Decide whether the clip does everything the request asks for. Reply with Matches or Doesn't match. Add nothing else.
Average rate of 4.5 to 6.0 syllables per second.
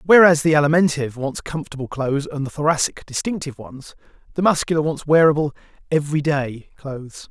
Doesn't match